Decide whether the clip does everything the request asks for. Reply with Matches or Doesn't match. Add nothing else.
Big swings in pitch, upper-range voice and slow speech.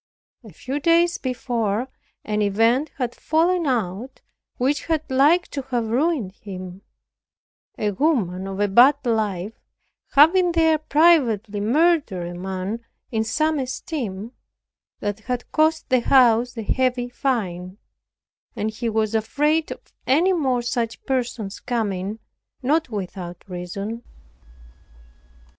Matches